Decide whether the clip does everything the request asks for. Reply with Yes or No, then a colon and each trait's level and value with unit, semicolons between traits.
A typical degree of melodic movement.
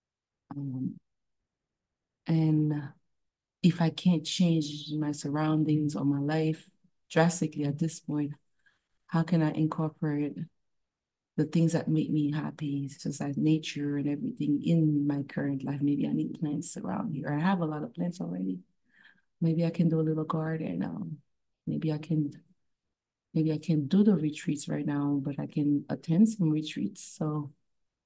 No: narrow, 2.1 semitones